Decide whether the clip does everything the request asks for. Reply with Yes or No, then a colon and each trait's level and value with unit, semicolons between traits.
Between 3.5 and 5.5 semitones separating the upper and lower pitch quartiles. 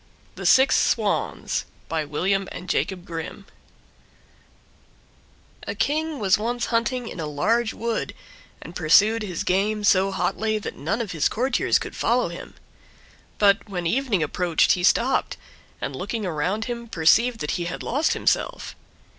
Yes: average, 4.8 semitones